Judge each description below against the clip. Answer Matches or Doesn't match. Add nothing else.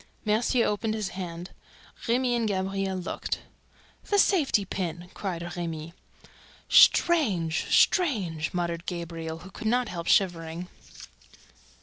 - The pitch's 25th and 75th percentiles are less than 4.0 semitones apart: Doesn't match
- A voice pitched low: Doesn't match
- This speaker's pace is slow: Matches